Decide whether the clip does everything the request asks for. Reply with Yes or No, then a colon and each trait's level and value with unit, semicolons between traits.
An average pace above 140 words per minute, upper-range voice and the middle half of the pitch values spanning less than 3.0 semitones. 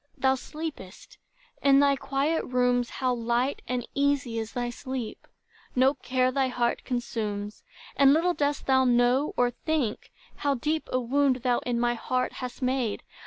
Yes: average, 160 wpm; very high, 255 Hz; narrow, 2.4 semitones